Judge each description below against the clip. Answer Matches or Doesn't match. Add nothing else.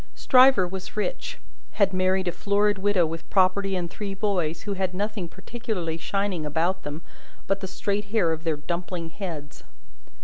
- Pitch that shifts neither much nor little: Matches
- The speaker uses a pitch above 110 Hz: Matches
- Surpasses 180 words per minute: Doesn't match